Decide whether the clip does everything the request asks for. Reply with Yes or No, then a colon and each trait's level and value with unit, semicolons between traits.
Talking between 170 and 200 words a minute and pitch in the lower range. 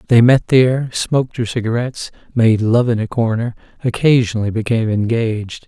No: average, 150 wpm; low, 115 Hz